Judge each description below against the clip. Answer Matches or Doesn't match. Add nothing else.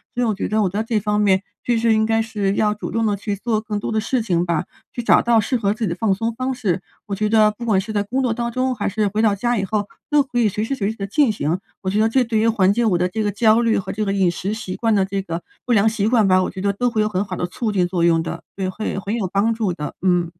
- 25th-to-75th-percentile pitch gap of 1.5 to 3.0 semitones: Matches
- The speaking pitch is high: Matches